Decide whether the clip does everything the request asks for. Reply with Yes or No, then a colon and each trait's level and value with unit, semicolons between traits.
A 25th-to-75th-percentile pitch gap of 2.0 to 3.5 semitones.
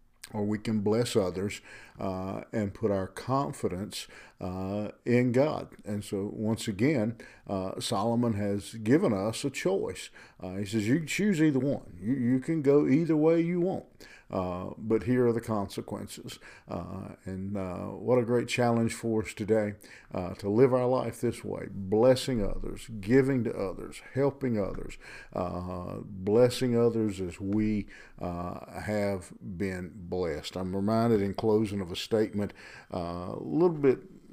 No: average, 4.0 semitones